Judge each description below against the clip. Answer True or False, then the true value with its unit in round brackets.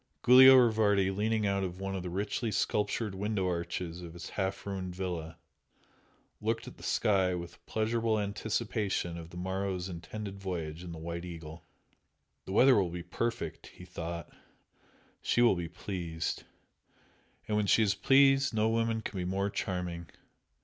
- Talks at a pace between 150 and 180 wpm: True (160 wpm)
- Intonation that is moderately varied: True (3.7 semitones)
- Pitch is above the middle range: False (95 Hz)